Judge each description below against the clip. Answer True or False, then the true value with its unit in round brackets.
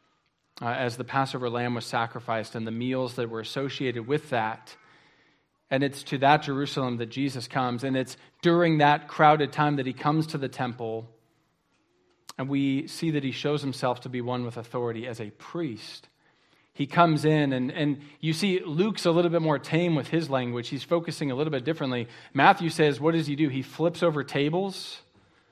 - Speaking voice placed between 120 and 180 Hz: True (140 Hz)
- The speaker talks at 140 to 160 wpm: False (195 wpm)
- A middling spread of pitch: True (3.8 semitones)